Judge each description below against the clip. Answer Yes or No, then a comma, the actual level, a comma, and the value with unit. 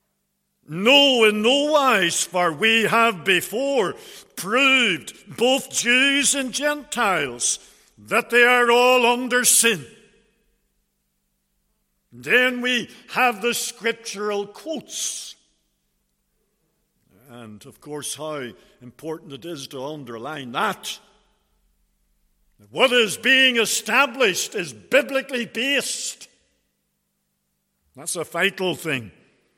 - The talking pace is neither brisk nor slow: No, slow, 95 wpm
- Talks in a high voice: Yes, high, 220 Hz